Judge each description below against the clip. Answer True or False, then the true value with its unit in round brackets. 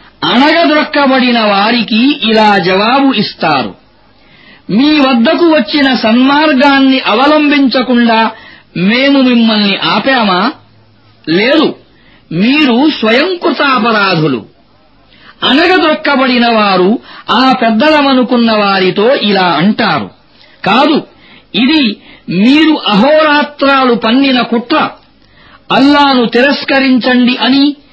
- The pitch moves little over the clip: False (4.3 semitones)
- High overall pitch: True (260 Hz)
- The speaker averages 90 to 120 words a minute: False (70 wpm)